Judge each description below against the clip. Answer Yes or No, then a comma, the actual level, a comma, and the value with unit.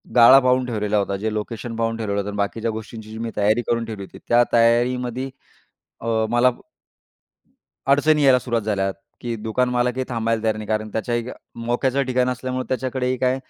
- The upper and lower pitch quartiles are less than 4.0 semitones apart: Yes, narrow, 2.5 semitones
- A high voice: No, low, 115 Hz